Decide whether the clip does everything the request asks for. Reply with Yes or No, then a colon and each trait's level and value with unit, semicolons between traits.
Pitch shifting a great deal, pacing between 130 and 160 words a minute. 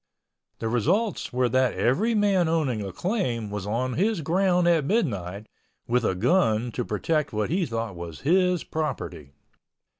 Yes: wide, 8.4 semitones; average, 155 wpm